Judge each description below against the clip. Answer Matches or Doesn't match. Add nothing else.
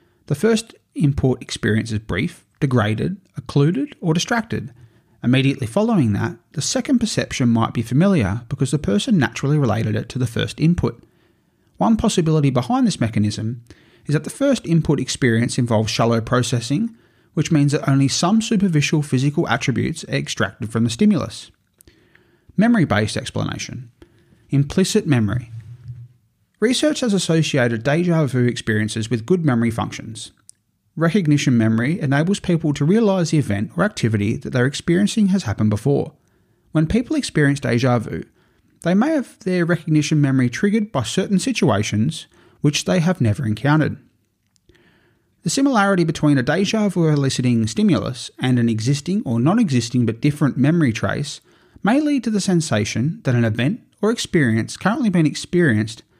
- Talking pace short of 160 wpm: Matches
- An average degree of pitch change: Doesn't match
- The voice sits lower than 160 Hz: Matches